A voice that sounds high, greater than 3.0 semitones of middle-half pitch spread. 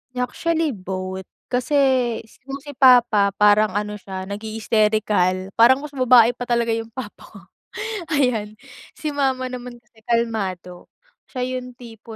Yes: high, 230 Hz; average, 3.4 semitones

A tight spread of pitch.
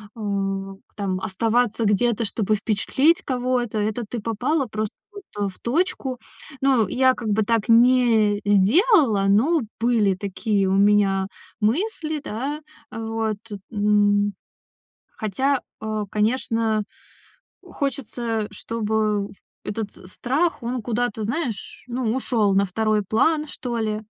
No: average, 3.3 semitones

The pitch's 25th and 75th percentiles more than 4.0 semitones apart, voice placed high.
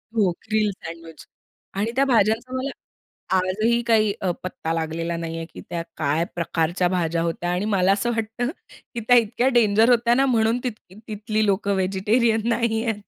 Yes: average, 4.7 semitones; high, 210 Hz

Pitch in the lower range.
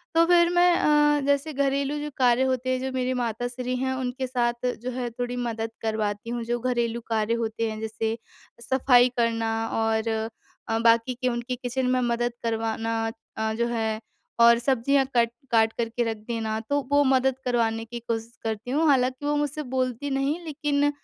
No: high, 245 Hz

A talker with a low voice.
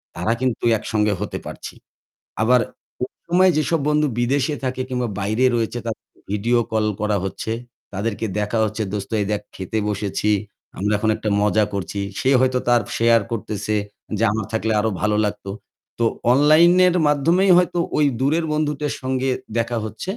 Yes: low, 115 Hz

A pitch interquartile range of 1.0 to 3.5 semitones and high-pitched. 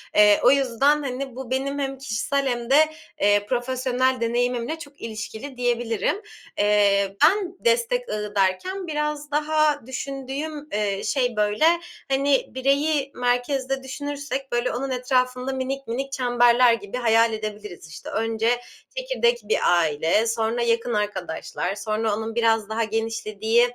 No: average, 3.9 semitones; high, 245 Hz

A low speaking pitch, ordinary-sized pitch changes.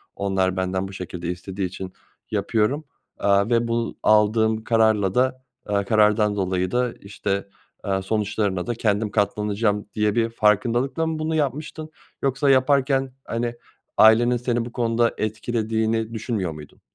Yes: low, 110 Hz; average, 3.1 semitones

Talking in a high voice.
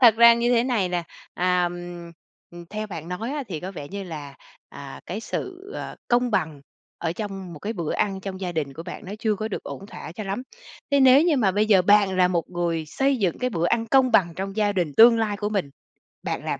Yes: high, 195 Hz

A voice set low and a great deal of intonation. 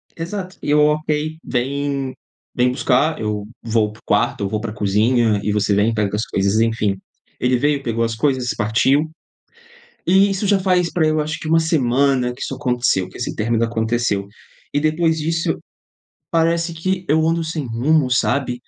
Yes: low, 130 Hz; wide, 5.8 semitones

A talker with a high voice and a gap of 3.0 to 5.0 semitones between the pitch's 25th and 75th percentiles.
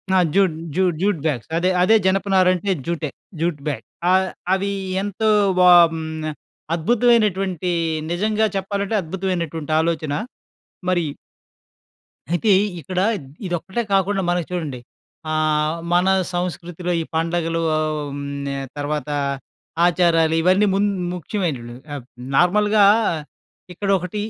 No: medium, 175 Hz; average, 3.4 semitones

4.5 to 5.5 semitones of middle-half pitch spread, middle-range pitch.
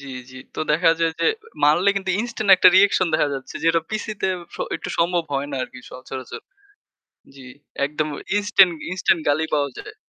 Yes: average, 5.0 semitones; medium, 165 Hz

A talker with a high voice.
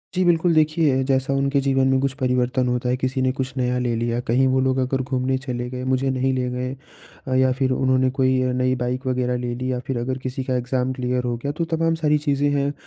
No: low, 130 Hz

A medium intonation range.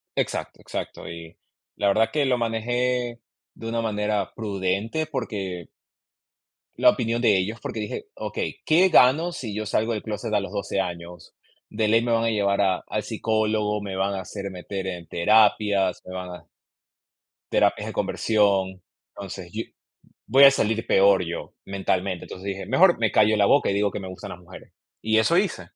Yes: average, 3.0 semitones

